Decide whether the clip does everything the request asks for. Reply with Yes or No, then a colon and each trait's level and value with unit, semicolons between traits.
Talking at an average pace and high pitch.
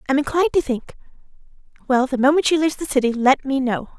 No: fast, 210 wpm; very high, 275 Hz